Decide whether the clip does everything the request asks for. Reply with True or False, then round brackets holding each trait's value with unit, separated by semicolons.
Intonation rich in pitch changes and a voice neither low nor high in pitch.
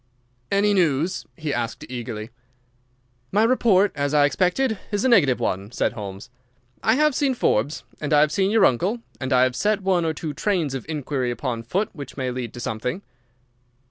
True (8.0 semitones; 150 Hz)